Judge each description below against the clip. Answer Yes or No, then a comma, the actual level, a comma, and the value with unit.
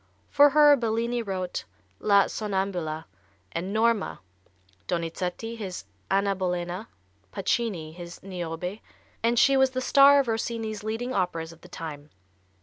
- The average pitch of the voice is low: No, high, 200 Hz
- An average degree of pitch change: Yes, average, 4.8 semitones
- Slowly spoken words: Yes, slow, 130 wpm